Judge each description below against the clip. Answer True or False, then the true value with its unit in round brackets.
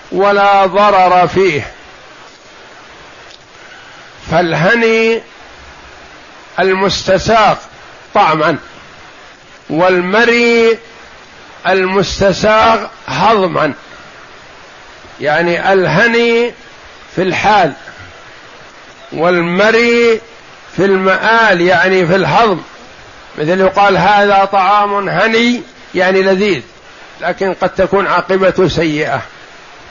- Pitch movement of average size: True (3.0 semitones)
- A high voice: True (195 Hz)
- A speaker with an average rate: False (60 wpm)